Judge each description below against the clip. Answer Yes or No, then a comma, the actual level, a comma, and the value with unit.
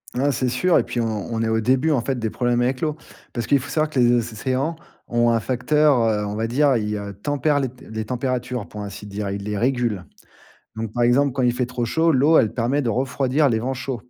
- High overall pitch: No, low, 125 Hz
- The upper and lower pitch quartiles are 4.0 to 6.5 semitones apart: No, average, 3.2 semitones